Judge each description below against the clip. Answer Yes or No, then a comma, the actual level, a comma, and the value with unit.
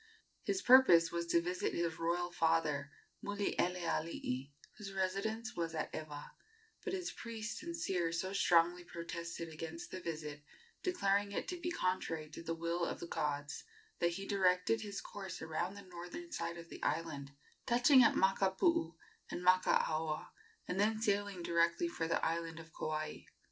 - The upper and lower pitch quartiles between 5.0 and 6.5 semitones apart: No, average, 3.4 semitones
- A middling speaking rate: Yes, average, 160 wpm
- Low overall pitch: No, medium, 175 Hz